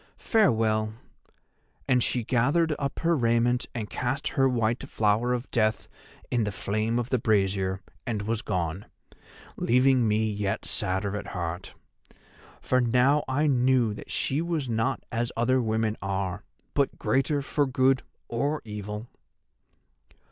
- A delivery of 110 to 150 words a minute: Yes, average, 140 wpm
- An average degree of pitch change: Yes, average, 3.7 semitones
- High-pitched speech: No, low, 115 Hz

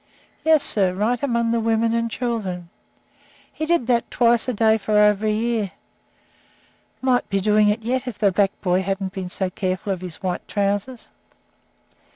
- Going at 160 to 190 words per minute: Yes, average, 175 wpm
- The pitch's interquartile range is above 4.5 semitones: No, average, 3.2 semitones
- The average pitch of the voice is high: Yes, high, 215 Hz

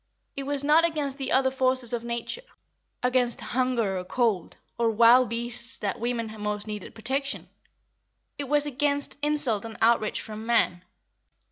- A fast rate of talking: No, average, 150 wpm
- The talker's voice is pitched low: No, high, 240 Hz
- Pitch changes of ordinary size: Yes, average, 3.5 semitones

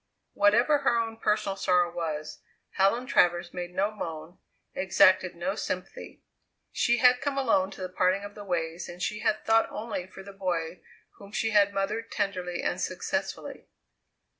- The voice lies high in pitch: Yes, high, 195 Hz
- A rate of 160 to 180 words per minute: Yes, average, 165 wpm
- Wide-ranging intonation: No, average, 3.3 semitones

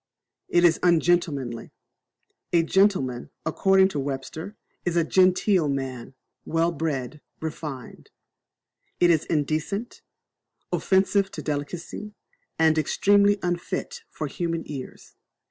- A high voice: No, medium, 165 Hz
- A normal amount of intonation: Yes, average, 4.5 semitones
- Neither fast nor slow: No, slow, 105 wpm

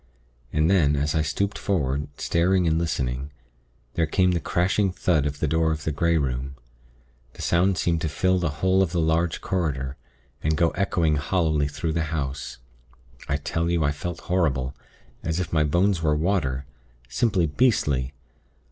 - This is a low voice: Yes, very low, 80 Hz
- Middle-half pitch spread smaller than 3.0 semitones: No, average, 3.4 semitones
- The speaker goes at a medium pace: Yes, average, 170 wpm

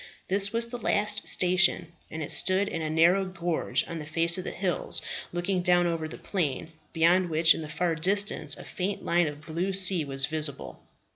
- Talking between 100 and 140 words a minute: No, average, 195 wpm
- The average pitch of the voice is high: No, medium, 175 Hz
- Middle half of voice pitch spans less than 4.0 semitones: Yes, average, 2.9 semitones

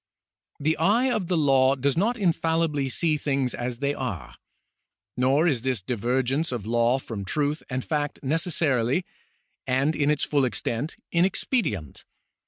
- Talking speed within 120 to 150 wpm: Yes, average, 145 wpm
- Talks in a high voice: No, medium, 140 Hz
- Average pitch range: Yes, average, 4.3 semitones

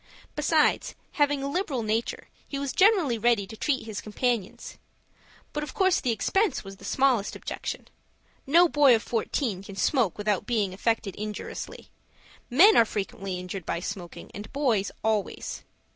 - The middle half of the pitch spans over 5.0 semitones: Yes, wide, 5.6 semitones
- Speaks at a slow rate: No, average, 155 wpm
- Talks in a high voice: Yes, high, 230 Hz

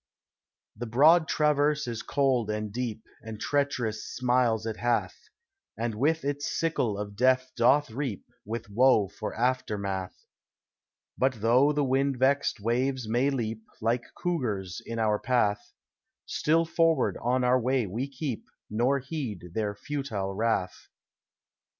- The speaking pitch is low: Yes, low, 120 Hz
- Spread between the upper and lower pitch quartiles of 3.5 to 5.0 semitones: Yes, average, 4.1 semitones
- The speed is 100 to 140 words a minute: Yes, slow, 135 wpm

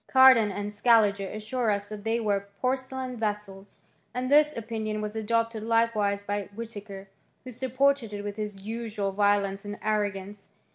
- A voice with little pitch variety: Yes, narrow, 2.3 semitones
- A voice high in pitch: Yes, high, 215 Hz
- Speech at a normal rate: Yes, average, 150 wpm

